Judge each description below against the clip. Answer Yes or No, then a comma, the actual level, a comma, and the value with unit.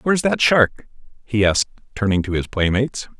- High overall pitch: No, low, 115 Hz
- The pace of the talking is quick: No, average, 170 wpm